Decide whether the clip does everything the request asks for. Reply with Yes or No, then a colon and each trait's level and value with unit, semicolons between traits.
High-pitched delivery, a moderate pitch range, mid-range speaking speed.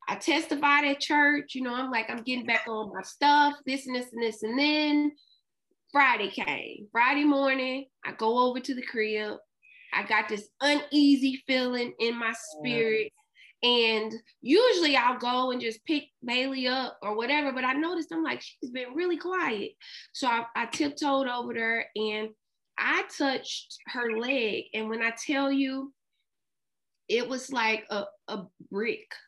Yes: very high, 260 Hz; average, 4.2 semitones; average, 165 wpm